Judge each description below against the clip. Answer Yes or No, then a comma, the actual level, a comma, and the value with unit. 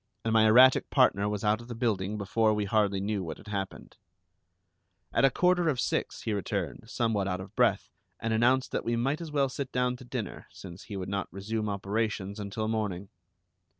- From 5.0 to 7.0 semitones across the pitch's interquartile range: No, average, 3.3 semitones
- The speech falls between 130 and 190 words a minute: No, average, 200 wpm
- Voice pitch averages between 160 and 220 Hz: No, low, 110 Hz